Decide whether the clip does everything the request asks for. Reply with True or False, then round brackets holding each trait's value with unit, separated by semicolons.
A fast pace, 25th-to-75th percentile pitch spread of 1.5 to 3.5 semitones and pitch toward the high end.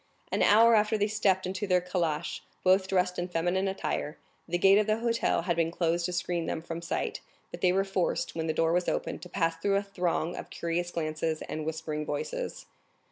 False (210 wpm; 2.8 semitones; 180 Hz)